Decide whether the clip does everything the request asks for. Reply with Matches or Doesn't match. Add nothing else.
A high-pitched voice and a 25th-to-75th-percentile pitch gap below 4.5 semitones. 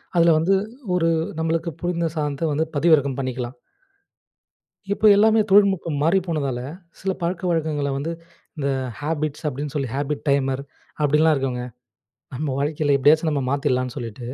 Doesn't match